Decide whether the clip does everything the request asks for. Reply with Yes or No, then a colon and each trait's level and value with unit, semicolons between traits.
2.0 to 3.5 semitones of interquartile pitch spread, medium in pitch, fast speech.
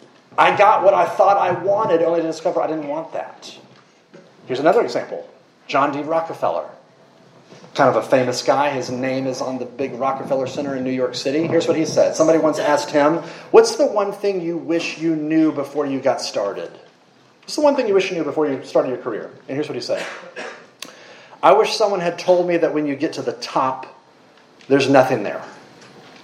No: average, 4.5 semitones; medium, 160 Hz; fast, 210 wpm